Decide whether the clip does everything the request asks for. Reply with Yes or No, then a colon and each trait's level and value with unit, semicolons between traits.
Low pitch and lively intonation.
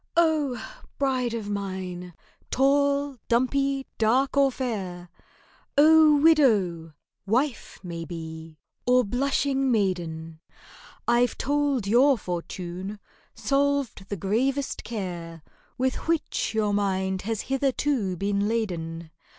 No: high, 225 Hz; wide, 6.8 semitones